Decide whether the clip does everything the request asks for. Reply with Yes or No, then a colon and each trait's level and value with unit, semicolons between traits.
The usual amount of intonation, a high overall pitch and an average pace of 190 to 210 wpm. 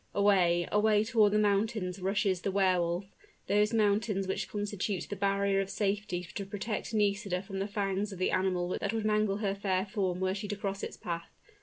No: narrow, 1.8 semitones; high, 200 Hz; average, 195 wpm